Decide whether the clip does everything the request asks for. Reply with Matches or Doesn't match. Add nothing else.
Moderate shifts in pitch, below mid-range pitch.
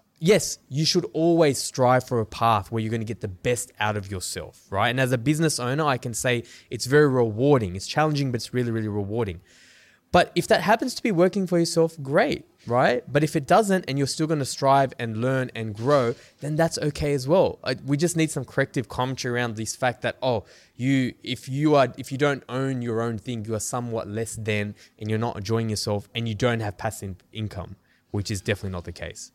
Matches